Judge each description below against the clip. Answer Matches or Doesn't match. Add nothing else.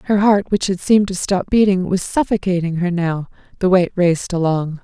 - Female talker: Matches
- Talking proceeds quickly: Matches